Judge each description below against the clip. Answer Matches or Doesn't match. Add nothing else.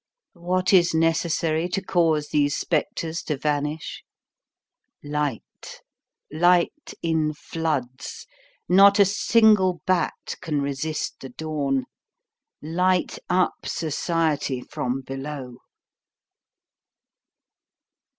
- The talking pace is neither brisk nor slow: Doesn't match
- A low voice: Doesn't match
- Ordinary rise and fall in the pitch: Matches